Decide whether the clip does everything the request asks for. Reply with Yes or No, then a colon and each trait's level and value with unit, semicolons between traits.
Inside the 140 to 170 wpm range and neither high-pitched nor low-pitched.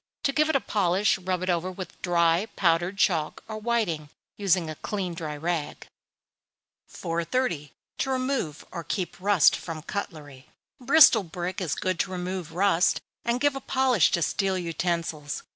Yes: average, 160 wpm; medium, 180 Hz